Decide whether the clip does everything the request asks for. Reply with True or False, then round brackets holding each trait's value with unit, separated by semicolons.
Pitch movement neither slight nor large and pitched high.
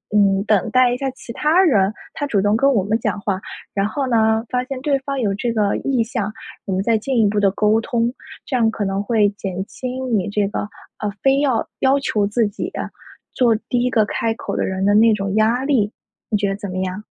True (3.8 semitones; 220 Hz)